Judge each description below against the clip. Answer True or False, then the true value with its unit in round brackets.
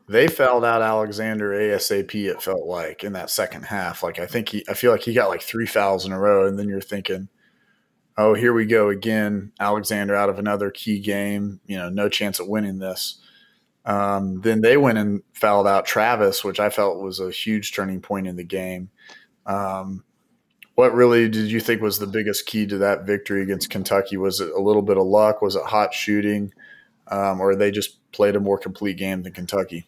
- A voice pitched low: True (100 Hz)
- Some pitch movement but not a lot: False (1.5 semitones)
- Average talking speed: False (210 wpm)